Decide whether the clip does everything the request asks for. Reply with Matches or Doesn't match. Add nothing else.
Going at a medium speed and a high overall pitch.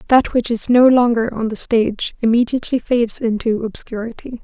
Matches